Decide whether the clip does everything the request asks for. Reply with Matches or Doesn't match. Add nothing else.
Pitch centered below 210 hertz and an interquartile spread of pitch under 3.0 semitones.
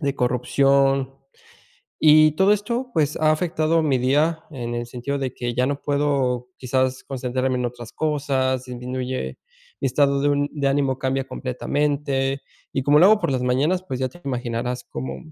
Matches